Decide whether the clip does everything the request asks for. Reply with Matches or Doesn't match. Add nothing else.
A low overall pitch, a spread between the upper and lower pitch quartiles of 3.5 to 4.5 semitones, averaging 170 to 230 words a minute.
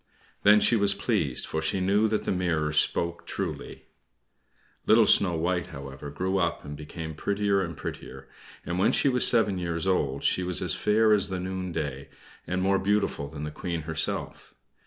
Matches